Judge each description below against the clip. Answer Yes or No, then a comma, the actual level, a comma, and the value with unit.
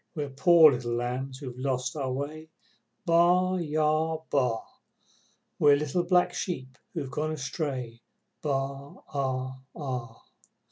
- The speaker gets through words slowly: Yes, slow, 120 wpm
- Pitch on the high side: No, medium, 140 Hz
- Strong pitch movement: No, average, 3.3 semitones